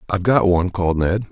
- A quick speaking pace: Yes, fast, 230 wpm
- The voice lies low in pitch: Yes, very low, 95 Hz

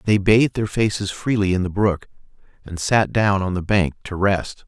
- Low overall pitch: Yes, low, 100 Hz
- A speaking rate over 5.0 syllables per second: No, 4.8 syllables/s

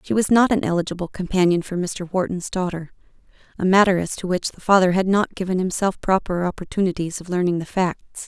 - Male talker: No, female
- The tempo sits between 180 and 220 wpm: Yes, average, 190 wpm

